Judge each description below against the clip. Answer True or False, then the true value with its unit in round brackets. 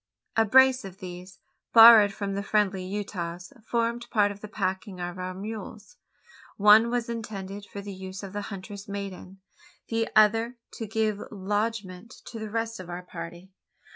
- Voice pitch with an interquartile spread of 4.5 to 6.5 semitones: False (3.0 semitones)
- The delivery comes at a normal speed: True (165 wpm)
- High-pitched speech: True (205 Hz)